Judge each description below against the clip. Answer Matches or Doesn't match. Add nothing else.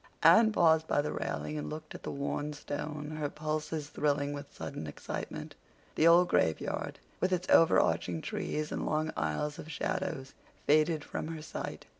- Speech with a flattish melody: Matches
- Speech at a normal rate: Matches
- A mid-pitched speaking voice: Matches